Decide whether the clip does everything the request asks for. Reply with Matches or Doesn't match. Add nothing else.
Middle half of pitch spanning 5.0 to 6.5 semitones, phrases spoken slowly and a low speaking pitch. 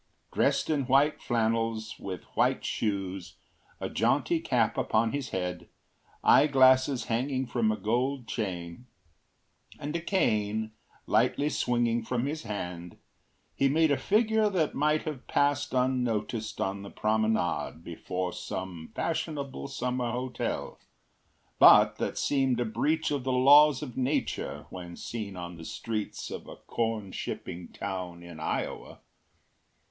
Matches